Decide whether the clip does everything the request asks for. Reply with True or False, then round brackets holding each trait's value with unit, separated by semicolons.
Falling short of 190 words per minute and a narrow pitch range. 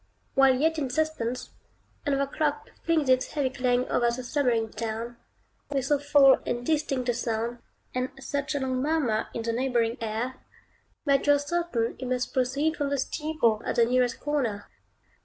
False (175 wpm; 3.3 semitones)